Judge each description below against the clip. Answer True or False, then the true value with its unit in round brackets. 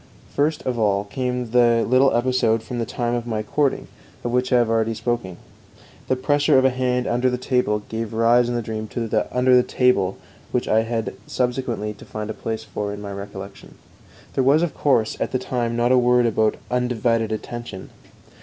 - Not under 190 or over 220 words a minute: True (200 wpm)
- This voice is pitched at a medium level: False (120 Hz)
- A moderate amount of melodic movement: False (2.3 semitones)